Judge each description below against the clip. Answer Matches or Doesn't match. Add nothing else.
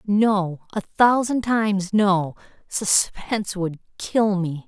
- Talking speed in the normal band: Doesn't match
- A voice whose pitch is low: Doesn't match